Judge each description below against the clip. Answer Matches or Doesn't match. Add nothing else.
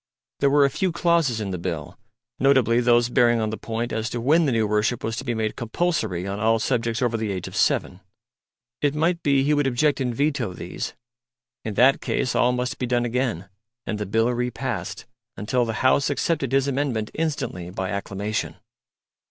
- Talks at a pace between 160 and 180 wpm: Doesn't match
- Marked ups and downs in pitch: Doesn't match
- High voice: Doesn't match